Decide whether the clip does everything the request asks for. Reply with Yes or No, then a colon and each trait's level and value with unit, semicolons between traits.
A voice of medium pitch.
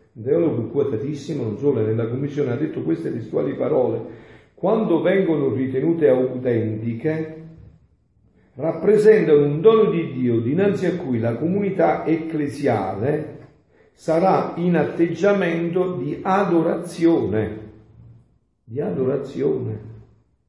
Yes: medium, 150 Hz